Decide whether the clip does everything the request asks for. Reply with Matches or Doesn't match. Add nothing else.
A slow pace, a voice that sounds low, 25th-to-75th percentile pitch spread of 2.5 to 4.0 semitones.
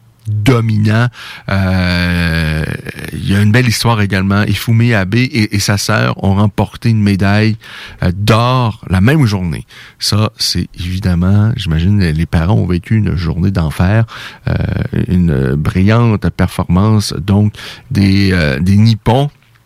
Matches